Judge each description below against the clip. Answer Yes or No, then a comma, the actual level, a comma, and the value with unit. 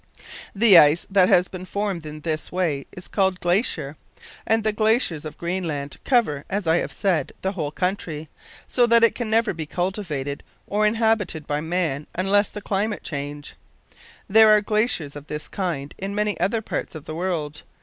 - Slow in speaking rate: No, average, 180 wpm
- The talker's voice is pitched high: No, medium, 180 Hz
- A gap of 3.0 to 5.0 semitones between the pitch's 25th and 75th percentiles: No, wide, 5.4 semitones